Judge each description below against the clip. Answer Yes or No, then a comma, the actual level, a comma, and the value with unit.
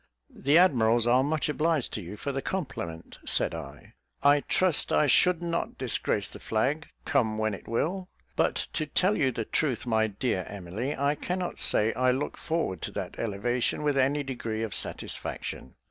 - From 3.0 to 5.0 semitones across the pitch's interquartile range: No, wide, 5.5 semitones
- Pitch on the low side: Yes, low, 130 Hz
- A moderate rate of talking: Yes, average, 175 wpm